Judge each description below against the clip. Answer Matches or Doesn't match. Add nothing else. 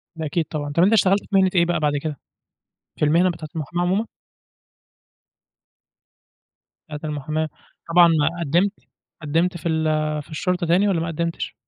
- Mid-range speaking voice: Matches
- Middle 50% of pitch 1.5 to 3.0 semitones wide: Matches